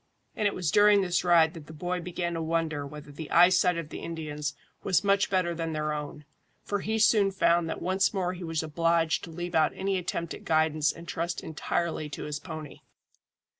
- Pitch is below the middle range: No, medium, 170 Hz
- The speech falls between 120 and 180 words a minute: No, fast, 205 wpm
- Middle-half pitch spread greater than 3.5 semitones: No, narrow, 2.5 semitones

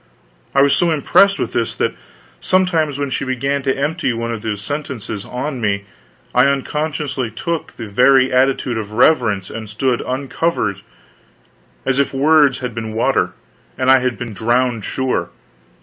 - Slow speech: No, average, 155 wpm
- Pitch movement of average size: Yes, average, 3.6 semitones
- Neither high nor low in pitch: No, low, 130 Hz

